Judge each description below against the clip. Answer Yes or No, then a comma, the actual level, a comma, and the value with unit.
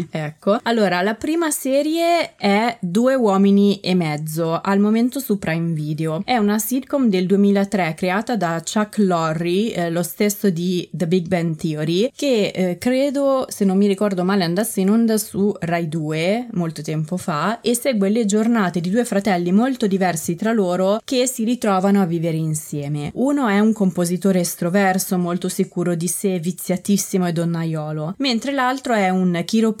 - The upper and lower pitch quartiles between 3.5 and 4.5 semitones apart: Yes, average, 4.2 semitones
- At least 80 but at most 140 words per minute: No, average, 165 wpm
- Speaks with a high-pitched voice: Yes, high, 195 Hz